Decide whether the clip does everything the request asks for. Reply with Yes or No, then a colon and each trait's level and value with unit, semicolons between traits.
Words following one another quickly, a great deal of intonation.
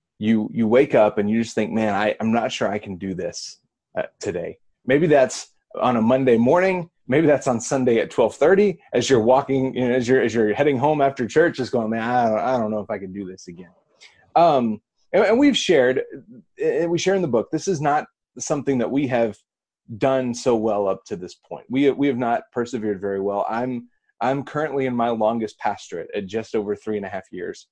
No: fast, 225 wpm; average, 4.8 semitones